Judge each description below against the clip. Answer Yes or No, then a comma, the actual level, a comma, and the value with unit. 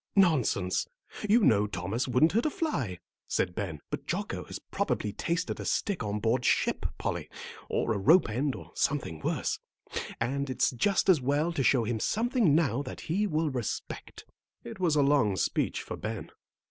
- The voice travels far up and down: Yes, wide, 7.4 semitones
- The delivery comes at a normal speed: Yes, average, 175 wpm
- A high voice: No, low, 135 Hz